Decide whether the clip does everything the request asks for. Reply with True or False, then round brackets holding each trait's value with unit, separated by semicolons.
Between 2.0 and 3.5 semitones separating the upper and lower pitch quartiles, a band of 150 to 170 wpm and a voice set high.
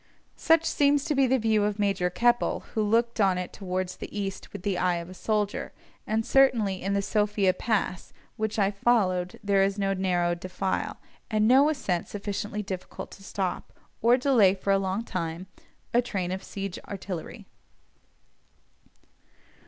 True (3.0 semitones; 160 wpm; 200 Hz)